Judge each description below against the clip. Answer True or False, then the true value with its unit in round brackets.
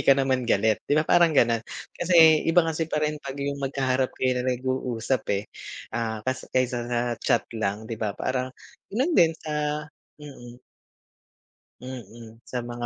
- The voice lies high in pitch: False (130 Hz)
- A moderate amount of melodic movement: True (4.0 semitones)